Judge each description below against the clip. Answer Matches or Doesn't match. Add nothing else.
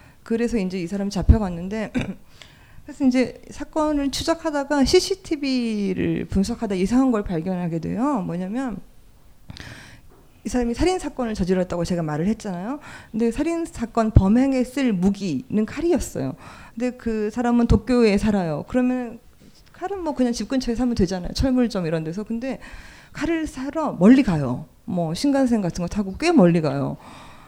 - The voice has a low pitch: Doesn't match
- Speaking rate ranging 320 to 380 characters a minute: Matches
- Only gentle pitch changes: Doesn't match